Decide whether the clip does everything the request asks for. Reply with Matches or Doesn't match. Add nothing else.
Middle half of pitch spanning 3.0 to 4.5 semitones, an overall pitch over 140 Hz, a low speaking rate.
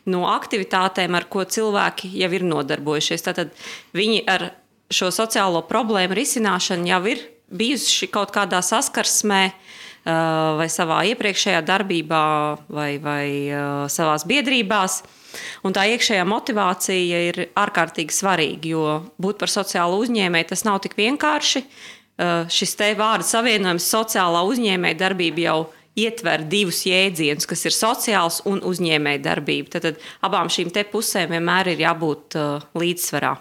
Matches